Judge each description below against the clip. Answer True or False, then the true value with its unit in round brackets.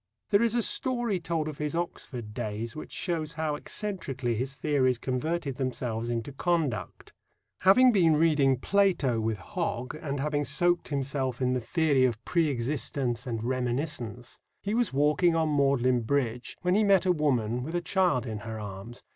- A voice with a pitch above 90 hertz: True (140 Hz)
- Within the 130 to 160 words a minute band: False (170 wpm)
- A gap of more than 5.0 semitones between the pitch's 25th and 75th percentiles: True (5.4 semitones)